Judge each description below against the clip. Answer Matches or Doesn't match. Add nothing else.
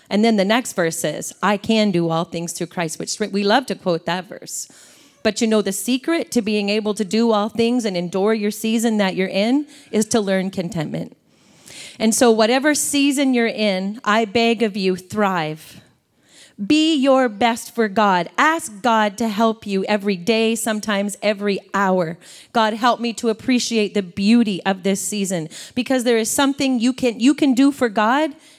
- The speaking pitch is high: Matches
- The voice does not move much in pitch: Doesn't match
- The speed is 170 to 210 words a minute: Matches